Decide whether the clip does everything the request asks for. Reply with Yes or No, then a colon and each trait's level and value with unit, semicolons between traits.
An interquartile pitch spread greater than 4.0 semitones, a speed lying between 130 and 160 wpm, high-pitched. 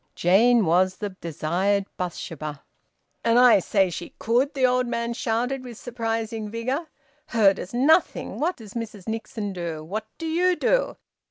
Yes: average, 4.6 semitones; average, 155 wpm; high, 225 Hz